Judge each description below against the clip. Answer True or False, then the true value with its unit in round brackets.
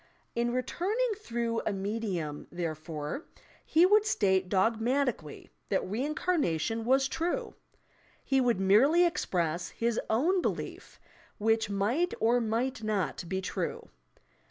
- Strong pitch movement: True (6.2 semitones)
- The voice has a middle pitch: False (225 Hz)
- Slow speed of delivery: True (115 wpm)